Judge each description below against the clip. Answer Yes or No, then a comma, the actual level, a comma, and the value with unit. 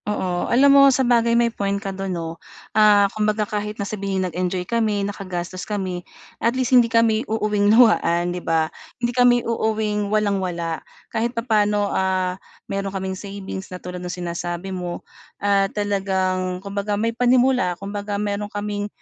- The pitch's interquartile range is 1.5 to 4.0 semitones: Yes, average, 2.8 semitones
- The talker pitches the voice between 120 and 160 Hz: No, high, 205 Hz